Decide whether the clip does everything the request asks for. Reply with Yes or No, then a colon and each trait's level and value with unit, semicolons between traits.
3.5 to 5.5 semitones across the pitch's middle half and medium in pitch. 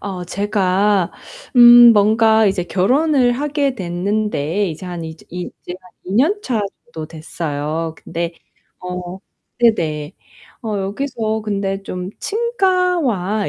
No: average, 5.2 semitones; high, 200 Hz